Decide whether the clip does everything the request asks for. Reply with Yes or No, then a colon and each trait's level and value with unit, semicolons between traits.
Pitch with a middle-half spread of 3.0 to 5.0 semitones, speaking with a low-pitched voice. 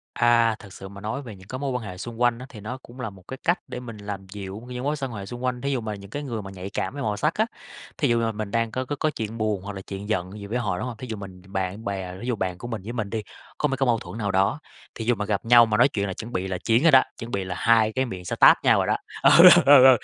Yes: average, 3.9 semitones; low, 110 Hz